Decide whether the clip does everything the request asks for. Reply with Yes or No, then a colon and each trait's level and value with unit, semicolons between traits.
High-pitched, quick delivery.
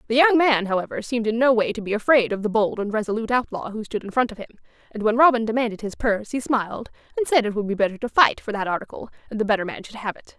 Yes: high, 225 Hz; fast, 285 wpm